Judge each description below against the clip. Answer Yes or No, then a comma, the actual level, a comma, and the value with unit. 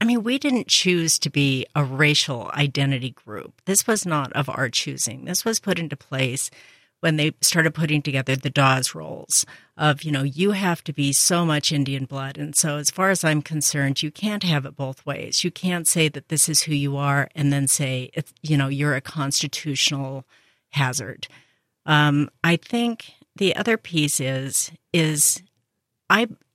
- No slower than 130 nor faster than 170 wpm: No, average, 185 wpm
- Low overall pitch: No, medium, 150 Hz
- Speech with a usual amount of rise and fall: Yes, average, 3.4 semitones